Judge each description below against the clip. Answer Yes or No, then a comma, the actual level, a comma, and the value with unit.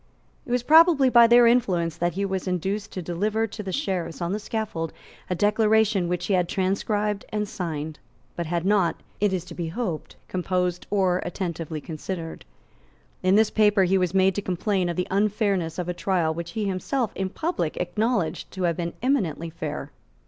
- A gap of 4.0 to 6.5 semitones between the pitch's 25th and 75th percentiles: No, average, 3.5 semitones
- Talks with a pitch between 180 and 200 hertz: Yes, high, 190 Hz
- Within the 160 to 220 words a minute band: Yes, average, 190 wpm